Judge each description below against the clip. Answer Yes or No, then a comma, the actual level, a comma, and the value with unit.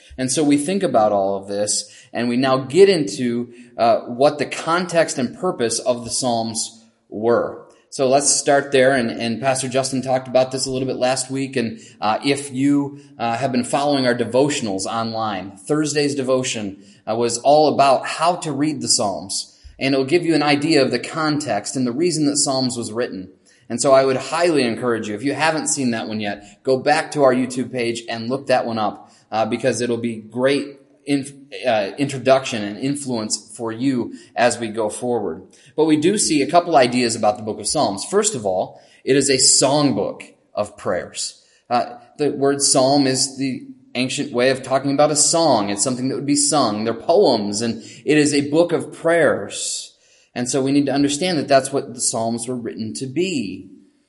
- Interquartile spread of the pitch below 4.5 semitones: Yes, average, 3.5 semitones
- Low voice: Yes, low, 130 Hz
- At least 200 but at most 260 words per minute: Yes, fast, 205 wpm